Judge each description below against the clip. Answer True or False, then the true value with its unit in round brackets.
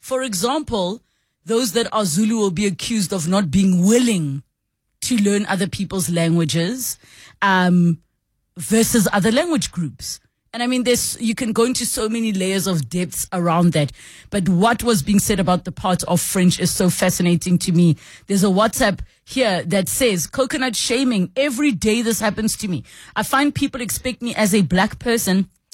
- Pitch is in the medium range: False (200 Hz)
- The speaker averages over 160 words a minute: True (175 wpm)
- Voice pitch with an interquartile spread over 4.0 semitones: True (4.5 semitones)